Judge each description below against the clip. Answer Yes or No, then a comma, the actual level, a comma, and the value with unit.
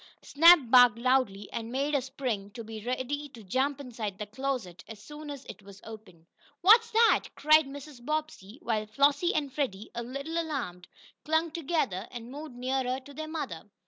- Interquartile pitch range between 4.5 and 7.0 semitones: Yes, average, 5.1 semitones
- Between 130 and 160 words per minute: No, average, 175 wpm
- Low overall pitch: No, very high, 260 Hz